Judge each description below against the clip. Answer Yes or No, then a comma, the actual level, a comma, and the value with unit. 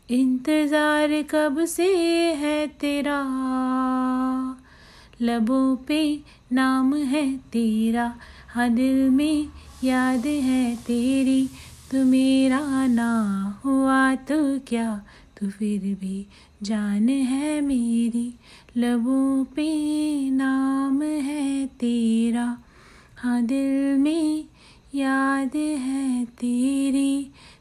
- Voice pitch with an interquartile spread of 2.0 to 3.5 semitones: Yes, average, 2.8 semitones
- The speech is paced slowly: Yes, slow, 90 wpm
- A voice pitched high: Yes, very high, 265 Hz